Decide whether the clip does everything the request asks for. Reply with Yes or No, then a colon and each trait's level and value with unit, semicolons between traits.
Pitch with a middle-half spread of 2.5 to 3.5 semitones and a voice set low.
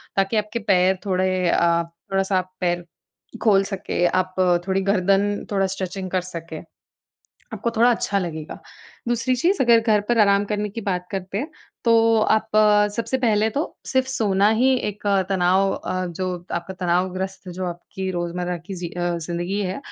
No: average, 2.9 semitones; high, 190 Hz